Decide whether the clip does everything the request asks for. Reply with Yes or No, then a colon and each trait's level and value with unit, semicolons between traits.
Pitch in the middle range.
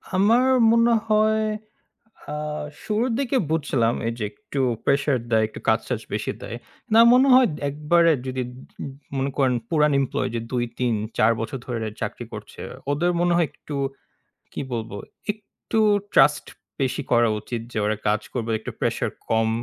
Yes: medium, 145 Hz